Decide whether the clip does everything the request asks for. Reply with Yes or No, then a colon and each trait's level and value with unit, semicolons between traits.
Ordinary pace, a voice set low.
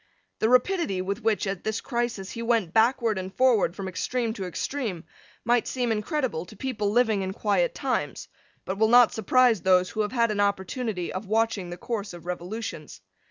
No: average, 185 wpm; high, 215 Hz